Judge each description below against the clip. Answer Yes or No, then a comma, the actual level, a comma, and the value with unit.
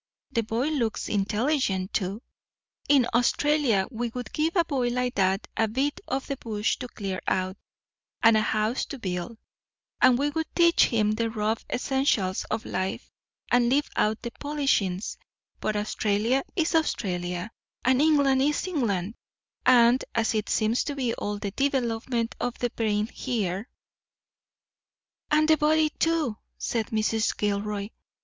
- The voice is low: No, high, 230 Hz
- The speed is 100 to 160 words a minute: Yes, average, 150 wpm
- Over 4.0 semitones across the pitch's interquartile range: Yes, average, 4.6 semitones